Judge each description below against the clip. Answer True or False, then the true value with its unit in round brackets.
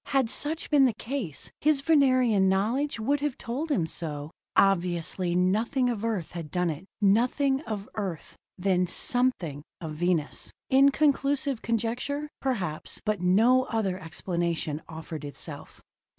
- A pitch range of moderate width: False (7.2 semitones)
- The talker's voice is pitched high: True (215 Hz)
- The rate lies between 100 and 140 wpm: True (135 wpm)